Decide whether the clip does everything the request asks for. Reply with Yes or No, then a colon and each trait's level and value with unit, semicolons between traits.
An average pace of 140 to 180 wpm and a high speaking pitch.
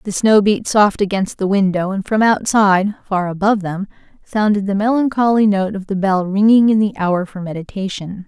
No: average, 190 wpm; high, 200 Hz